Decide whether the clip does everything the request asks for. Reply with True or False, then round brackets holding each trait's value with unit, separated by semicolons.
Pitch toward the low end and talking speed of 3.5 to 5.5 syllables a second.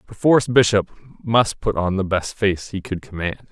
True (100 Hz; 5.0 syllables/s)